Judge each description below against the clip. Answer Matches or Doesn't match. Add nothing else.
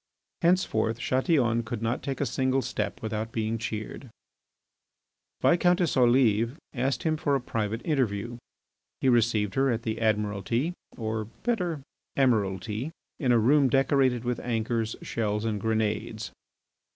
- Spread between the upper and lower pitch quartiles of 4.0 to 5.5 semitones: Doesn't match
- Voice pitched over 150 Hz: Doesn't match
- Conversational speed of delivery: Doesn't match